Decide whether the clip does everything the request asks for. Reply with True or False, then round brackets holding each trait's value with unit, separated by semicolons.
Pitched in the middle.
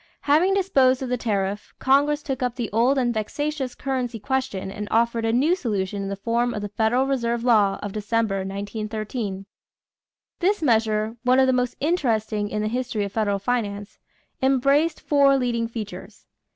False (235 Hz)